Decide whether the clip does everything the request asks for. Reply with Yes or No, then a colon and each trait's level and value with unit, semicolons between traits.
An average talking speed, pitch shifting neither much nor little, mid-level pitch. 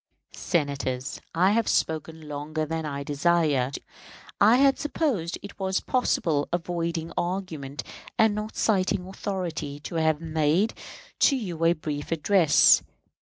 No: slow, 125 wpm; average, 4.2 semitones; medium, 165 Hz